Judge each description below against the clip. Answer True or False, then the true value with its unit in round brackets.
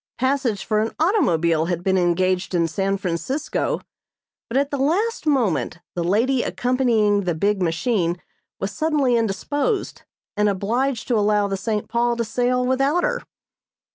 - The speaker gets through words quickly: False (150 wpm)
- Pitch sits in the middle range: False (220 Hz)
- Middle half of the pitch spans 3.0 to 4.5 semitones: False (5.6 semitones)